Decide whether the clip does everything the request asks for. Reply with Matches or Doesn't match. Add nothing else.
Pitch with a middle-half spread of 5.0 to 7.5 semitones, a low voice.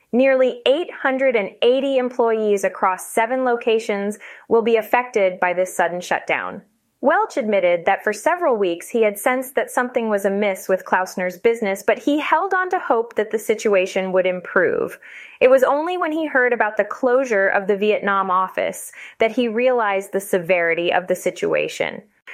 Doesn't match